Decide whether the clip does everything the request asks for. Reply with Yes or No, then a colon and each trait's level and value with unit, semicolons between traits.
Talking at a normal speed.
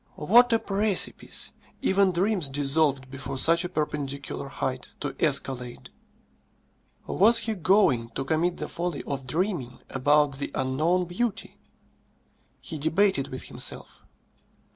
No: slow, 120 wpm